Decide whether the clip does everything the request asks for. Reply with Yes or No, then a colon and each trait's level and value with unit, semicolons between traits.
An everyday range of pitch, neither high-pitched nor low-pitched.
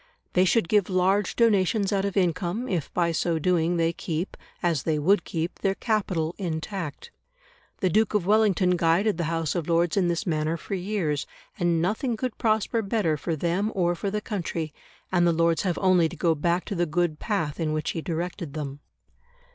Yes: average, 3.3 semitones; medium, 175 Hz